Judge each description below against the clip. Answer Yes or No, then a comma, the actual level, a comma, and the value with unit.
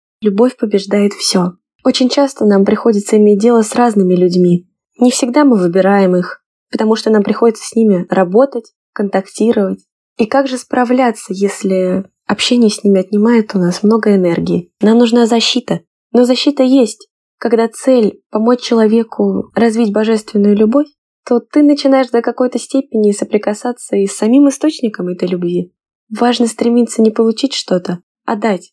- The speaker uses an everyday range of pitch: Yes, average, 3.5 semitones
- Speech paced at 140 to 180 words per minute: Yes, average, 150 wpm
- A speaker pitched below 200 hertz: No, high, 225 Hz